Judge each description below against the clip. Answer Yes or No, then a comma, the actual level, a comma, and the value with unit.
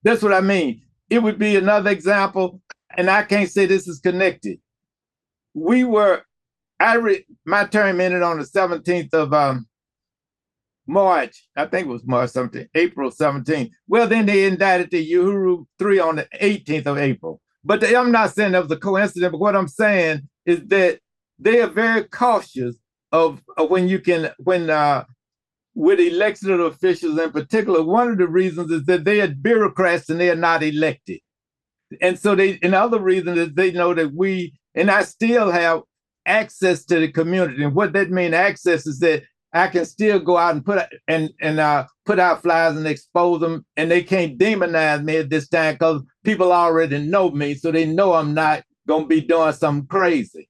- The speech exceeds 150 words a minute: Yes, average, 190 wpm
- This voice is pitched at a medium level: Yes, medium, 175 Hz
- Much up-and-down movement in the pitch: No, average, 3.8 semitones